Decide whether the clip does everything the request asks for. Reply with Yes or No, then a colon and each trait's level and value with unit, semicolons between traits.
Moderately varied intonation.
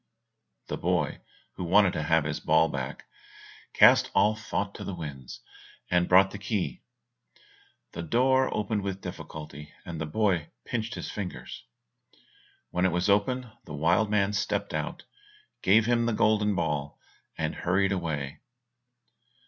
Yes: average, 4.6 semitones